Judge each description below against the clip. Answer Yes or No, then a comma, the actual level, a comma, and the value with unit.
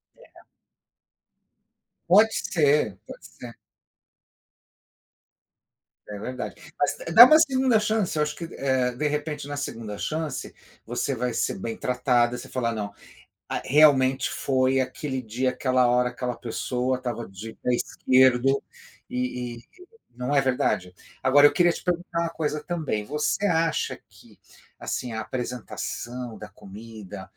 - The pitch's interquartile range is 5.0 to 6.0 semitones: No, average, 4.0 semitones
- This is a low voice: Yes, low, 130 Hz